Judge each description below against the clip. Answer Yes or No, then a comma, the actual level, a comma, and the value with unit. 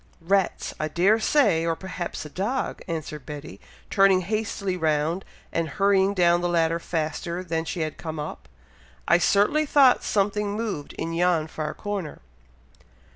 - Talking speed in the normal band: Yes, average, 150 wpm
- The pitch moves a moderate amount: Yes, average, 3.7 semitones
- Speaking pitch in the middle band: Yes, medium, 175 Hz